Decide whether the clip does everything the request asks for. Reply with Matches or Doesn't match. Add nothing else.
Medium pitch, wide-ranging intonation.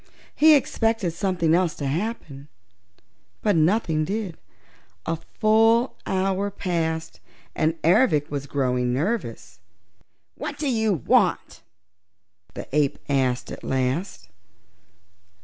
Matches